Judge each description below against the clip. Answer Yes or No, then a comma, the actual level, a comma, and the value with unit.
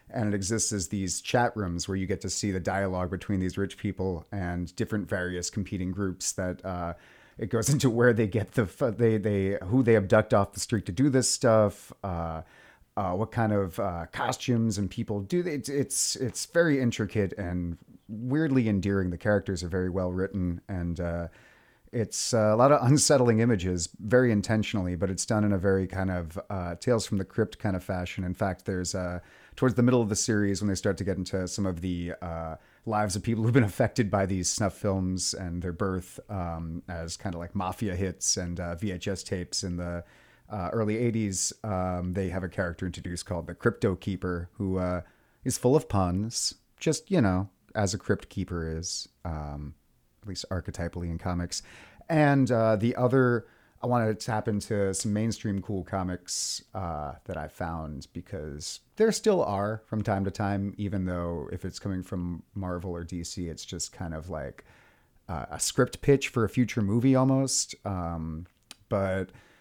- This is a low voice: Yes, low, 100 Hz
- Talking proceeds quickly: No, average, 190 wpm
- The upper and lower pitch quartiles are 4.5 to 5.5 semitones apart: No, average, 3.6 semitones